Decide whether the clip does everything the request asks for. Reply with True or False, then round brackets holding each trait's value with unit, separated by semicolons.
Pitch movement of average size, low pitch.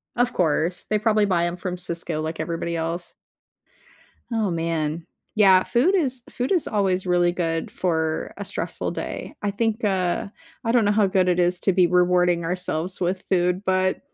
False (3.0 semitones; 180 Hz)